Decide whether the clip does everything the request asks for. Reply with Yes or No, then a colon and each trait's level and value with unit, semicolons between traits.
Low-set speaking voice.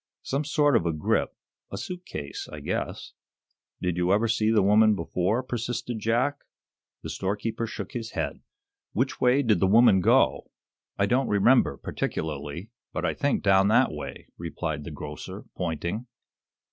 Yes: low, 105 Hz